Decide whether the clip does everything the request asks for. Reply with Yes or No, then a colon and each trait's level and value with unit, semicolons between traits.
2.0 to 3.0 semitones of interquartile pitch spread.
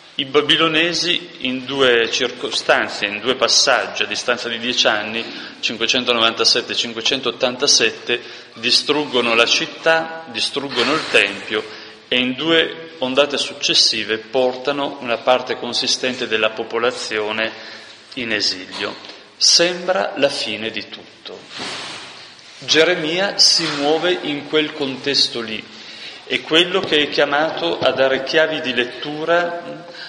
No: average, 4.8 semitones